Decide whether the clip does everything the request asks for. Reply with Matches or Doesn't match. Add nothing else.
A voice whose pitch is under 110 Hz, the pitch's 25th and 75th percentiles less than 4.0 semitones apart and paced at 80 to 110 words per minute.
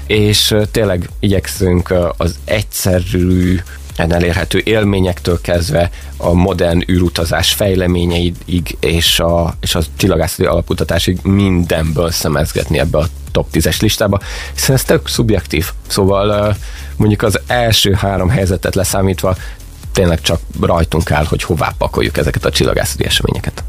Doesn't match